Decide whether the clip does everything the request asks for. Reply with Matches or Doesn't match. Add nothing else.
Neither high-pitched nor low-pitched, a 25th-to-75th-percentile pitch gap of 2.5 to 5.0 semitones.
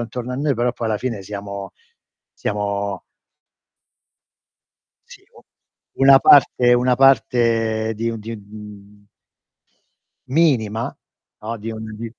Doesn't match